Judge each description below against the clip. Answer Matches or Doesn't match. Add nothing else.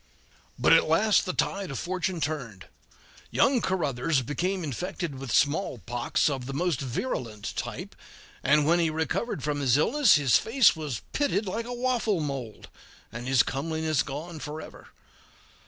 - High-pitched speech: Doesn't match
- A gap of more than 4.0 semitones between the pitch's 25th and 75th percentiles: Matches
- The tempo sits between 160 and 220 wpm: Doesn't match